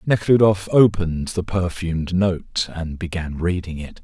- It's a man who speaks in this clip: Yes, male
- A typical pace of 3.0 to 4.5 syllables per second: Yes, 4.4 syllables/s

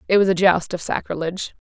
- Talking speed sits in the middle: No, fast, 220 wpm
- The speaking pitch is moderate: Yes, medium, 180 Hz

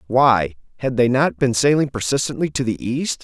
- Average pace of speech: Yes, average, 185 wpm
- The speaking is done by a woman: No, male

